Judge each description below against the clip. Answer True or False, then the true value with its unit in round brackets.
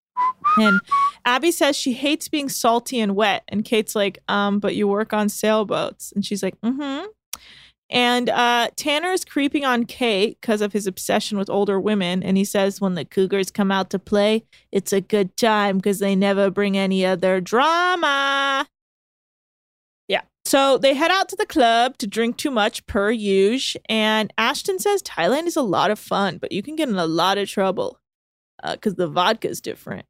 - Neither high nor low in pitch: False (215 Hz)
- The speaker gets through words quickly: False (190 wpm)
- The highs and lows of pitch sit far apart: True (5.7 semitones)